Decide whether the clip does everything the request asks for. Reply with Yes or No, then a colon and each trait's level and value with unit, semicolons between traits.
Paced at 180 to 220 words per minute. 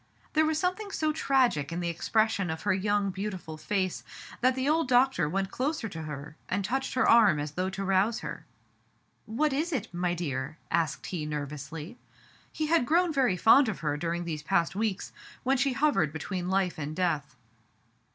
Yes: average, 185 wpm